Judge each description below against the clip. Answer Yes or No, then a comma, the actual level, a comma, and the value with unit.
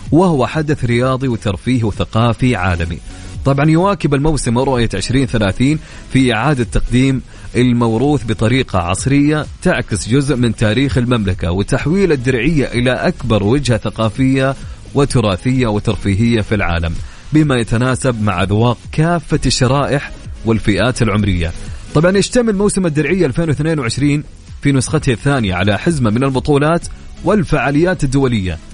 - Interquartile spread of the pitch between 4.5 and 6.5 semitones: Yes, average, 5.0 semitones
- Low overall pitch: Yes, low, 125 Hz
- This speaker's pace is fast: No, average, 115 wpm